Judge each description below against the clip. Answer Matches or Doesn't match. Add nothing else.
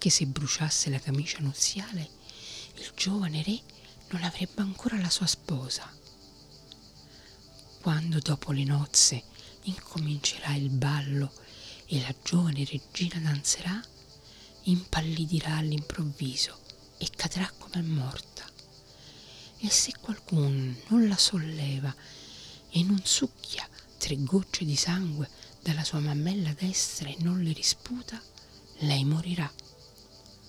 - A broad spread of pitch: Doesn't match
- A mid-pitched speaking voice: Matches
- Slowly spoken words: Matches